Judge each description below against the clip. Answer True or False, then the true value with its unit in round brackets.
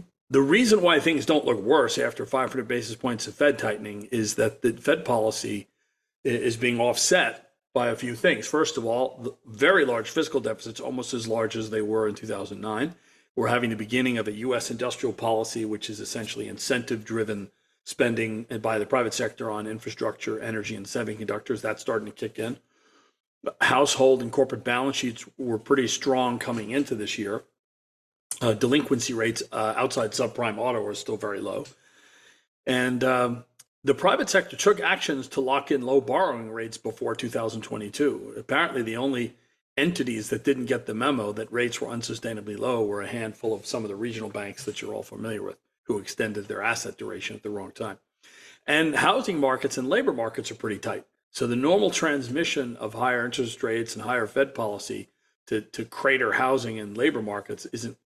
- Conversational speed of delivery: True (180 wpm)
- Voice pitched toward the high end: False (120 Hz)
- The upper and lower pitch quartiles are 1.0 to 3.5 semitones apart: True (2.9 semitones)